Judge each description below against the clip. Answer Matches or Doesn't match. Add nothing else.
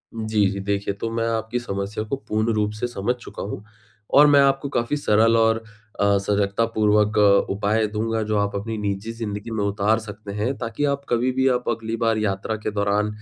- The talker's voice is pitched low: Matches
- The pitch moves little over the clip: Matches